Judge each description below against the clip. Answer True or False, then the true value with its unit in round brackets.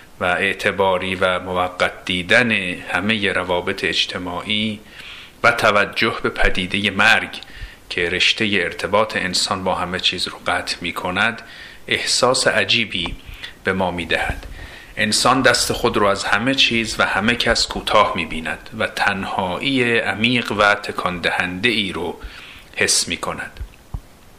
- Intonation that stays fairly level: False (3.9 semitones)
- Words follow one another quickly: False (135 wpm)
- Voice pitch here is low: True (105 Hz)